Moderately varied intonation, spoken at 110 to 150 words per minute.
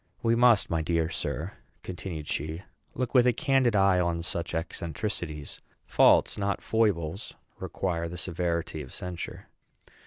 Yes: average, 4.0 semitones; slow, 135 wpm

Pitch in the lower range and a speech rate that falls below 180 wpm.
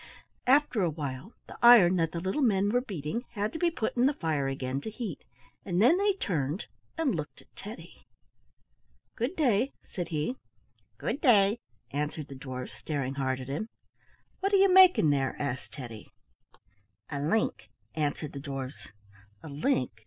No: medium, 175 Hz; average, 165 wpm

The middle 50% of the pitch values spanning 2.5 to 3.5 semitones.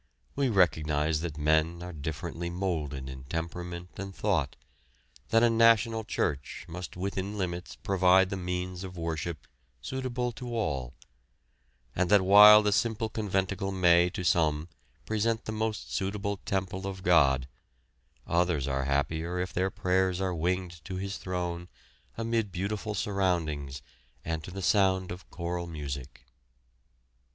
Yes: average, 3.2 semitones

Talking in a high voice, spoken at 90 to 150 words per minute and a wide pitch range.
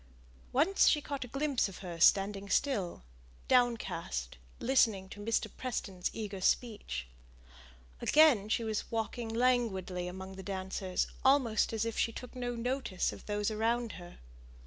No: high, 220 Hz; average, 145 wpm; average, 4.5 semitones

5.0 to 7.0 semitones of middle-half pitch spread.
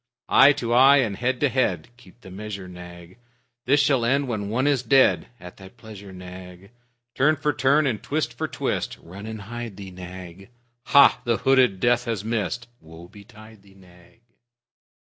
Yes: wide, 5.4 semitones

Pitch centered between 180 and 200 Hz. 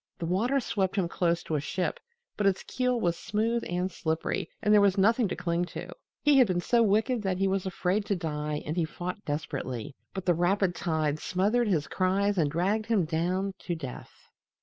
Yes: medium, 185 Hz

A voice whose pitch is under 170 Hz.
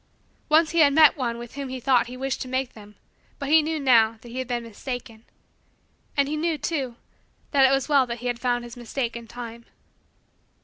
No: very high, 255 Hz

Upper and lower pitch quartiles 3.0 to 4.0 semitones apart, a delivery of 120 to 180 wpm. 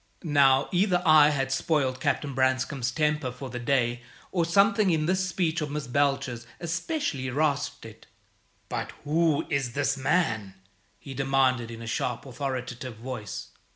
Yes: average, 3.7 semitones; average, 150 wpm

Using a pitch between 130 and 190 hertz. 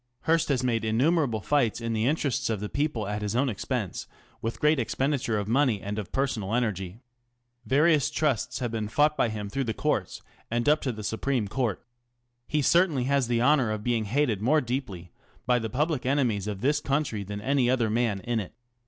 No: low, 120 Hz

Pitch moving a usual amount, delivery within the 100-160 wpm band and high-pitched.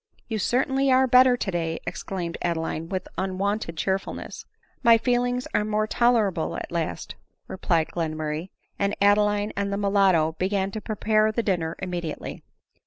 Yes: average, 4.1 semitones; average, 145 wpm; high, 200 Hz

